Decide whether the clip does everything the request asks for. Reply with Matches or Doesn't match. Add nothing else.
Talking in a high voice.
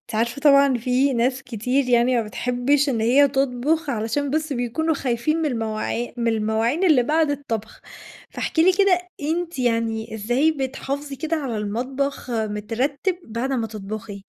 Matches